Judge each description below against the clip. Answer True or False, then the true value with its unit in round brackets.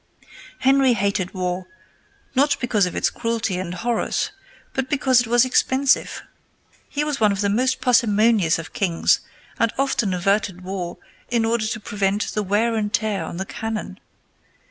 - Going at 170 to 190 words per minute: False (160 wpm)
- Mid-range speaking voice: False (215 Hz)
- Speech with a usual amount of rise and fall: True (4.0 semitones)